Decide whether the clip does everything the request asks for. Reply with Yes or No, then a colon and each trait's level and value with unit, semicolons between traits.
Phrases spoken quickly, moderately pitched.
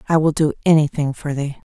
Yes: fast, 210 wpm; medium, 150 Hz